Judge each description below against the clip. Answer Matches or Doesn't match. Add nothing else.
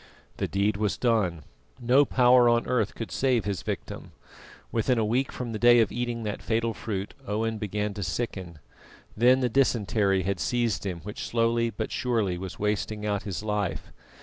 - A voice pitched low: Matches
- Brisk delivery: Doesn't match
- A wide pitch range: Doesn't match